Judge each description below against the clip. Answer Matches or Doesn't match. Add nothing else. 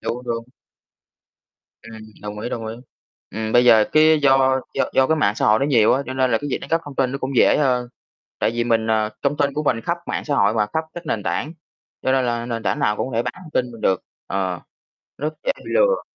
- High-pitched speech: Doesn't match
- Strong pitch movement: Doesn't match